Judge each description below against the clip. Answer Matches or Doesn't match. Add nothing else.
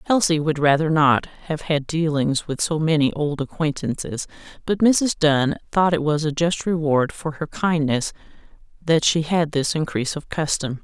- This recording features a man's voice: Doesn't match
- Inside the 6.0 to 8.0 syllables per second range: Doesn't match